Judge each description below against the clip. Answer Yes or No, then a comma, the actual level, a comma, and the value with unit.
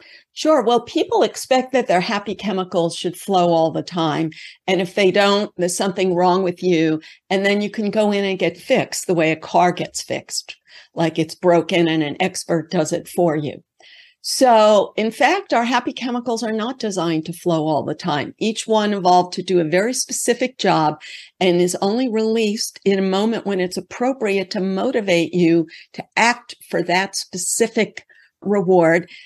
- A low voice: No, high, 190 Hz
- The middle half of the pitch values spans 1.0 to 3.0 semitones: No, average, 4.1 semitones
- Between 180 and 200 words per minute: Yes, average, 185 wpm